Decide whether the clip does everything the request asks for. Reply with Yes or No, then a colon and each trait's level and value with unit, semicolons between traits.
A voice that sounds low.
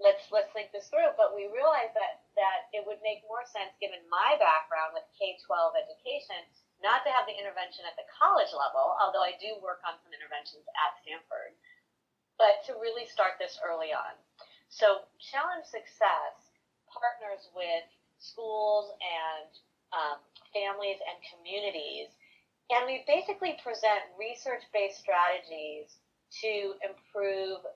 No: high, 210 Hz